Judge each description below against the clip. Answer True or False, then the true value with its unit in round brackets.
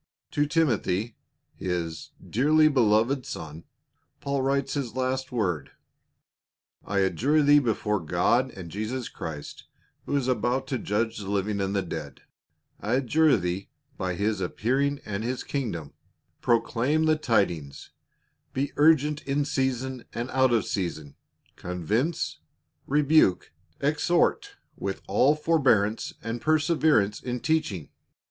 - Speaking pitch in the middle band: False (120 Hz)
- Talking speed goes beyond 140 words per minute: False (135 wpm)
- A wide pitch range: True (6.1 semitones)